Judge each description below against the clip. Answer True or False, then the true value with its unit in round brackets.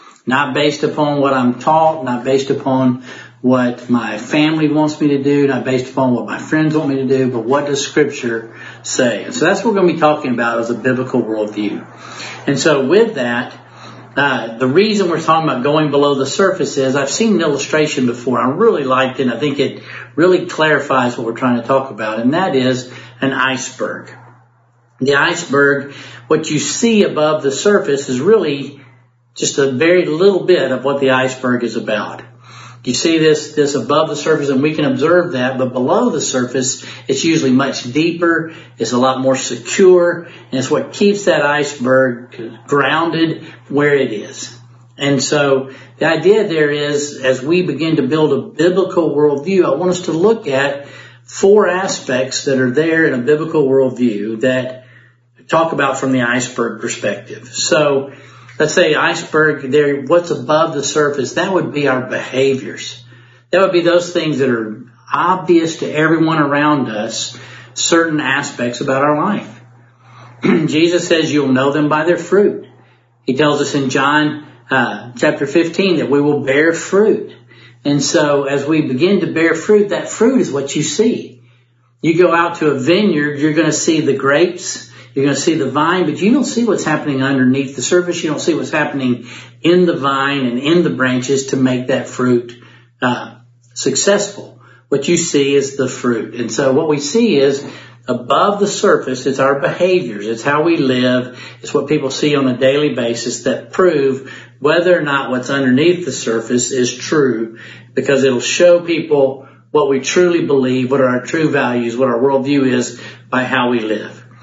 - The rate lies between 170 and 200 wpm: True (185 wpm)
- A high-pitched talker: False (140 Hz)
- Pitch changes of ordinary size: True (3.7 semitones)